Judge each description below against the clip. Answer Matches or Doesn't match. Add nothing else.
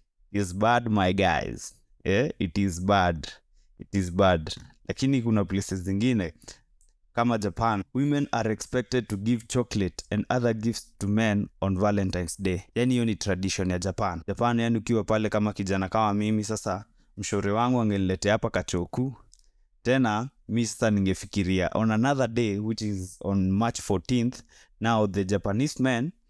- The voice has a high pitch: Doesn't match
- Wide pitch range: Doesn't match